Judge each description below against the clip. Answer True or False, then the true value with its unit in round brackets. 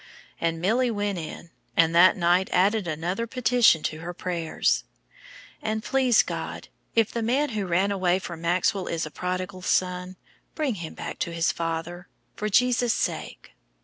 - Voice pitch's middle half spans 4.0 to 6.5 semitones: True (4.4 semitones)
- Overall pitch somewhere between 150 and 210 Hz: True (185 Hz)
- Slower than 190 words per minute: True (160 wpm)